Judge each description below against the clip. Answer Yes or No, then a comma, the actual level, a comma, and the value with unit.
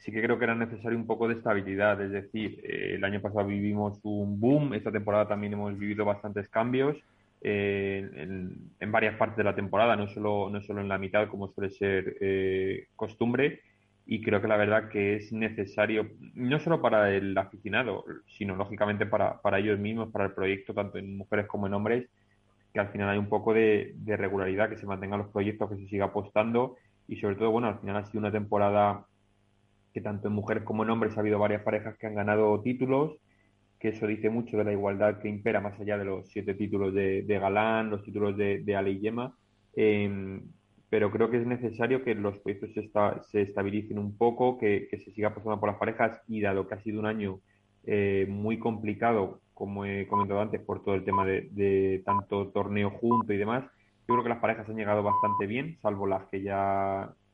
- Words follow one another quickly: Yes, fast, 210 wpm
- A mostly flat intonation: Yes, narrow, 1.5 semitones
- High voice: No, low, 105 Hz